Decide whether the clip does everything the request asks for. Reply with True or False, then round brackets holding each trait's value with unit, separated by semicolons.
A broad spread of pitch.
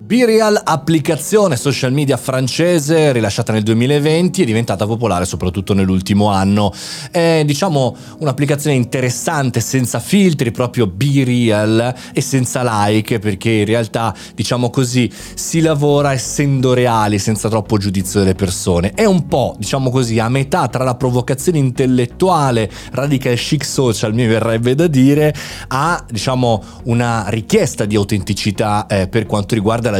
False (4.5 semitones)